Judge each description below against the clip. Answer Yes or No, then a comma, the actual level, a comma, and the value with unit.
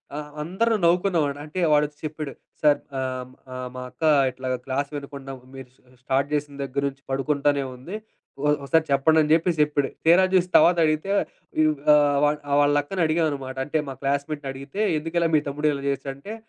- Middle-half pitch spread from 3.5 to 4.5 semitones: No, narrow, 2.5 semitones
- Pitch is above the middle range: No, medium, 145 Hz